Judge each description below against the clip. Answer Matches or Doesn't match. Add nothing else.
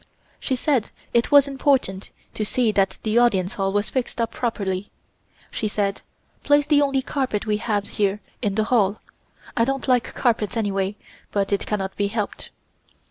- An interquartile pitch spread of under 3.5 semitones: Doesn't match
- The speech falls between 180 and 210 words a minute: Doesn't match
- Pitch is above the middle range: Matches